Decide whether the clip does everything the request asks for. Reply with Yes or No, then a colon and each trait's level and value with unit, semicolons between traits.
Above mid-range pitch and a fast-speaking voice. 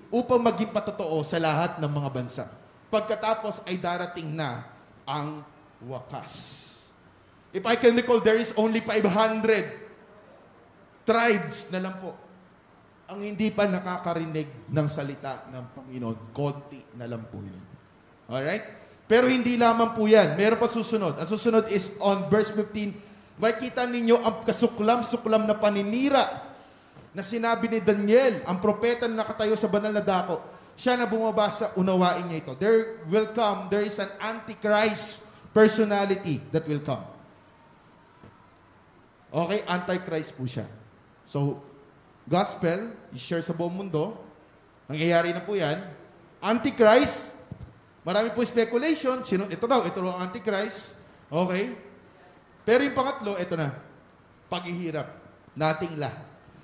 No: high, 200 Hz; average, 130 wpm